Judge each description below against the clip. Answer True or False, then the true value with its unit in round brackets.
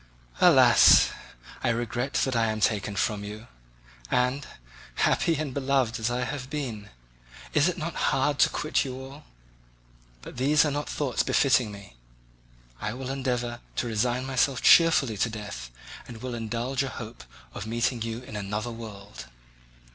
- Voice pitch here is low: True (120 Hz)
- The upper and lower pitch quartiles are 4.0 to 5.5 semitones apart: False (3.5 semitones)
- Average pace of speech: True (155 wpm)